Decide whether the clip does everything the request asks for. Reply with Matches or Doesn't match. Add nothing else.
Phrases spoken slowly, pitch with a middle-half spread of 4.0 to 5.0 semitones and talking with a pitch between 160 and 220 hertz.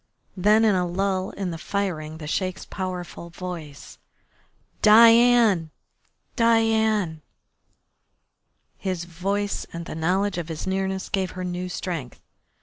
Doesn't match